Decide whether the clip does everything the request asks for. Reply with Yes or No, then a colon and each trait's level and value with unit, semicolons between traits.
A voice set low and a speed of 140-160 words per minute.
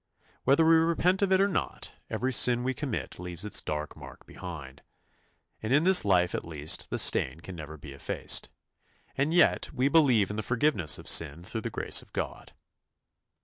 No: low, 110 Hz; average, 190 wpm